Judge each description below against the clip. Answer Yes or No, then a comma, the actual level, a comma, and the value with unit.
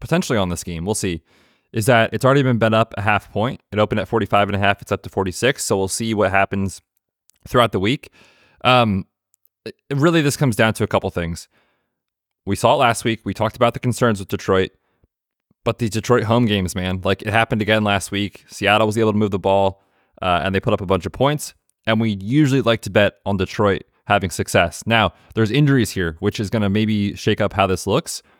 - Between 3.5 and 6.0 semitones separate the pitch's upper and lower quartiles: No, average, 2.9 semitones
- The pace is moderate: No, fast, 230 wpm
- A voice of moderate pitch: No, low, 105 Hz